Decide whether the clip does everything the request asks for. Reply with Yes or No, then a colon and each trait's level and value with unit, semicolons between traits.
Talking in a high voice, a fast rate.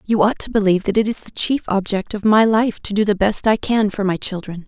Yes: high, 205 Hz; fast, 280 wpm